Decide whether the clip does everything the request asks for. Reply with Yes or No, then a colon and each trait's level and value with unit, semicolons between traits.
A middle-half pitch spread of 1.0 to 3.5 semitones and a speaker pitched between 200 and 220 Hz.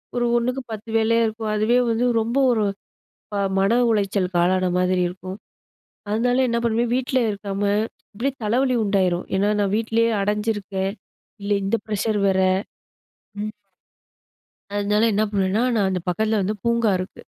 Yes: average, 2.8 semitones; high, 210 Hz